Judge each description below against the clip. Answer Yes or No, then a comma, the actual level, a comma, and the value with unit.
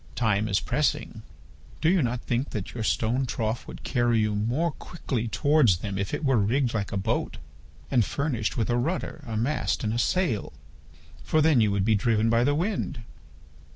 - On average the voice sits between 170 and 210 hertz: No, low, 120 Hz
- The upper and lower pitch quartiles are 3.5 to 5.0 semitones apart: Yes, average, 4.6 semitones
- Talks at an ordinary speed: Yes, average, 190 wpm